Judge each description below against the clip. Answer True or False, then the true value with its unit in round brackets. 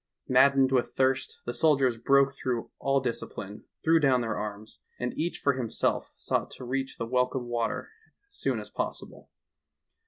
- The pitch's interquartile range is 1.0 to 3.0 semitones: True (2.4 semitones)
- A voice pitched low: True (130 Hz)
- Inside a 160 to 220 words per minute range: True (175 wpm)